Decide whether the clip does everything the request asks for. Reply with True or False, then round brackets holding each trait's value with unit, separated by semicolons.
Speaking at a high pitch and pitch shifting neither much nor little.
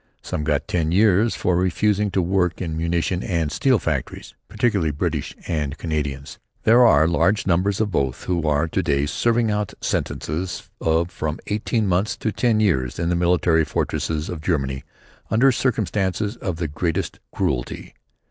False (85 Hz; 4.7 semitones)